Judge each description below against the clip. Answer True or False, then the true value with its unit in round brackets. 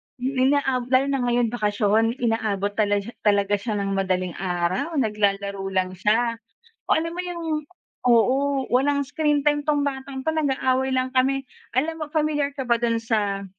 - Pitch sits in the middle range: False (250 Hz)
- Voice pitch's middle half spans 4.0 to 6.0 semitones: True (5.2 semitones)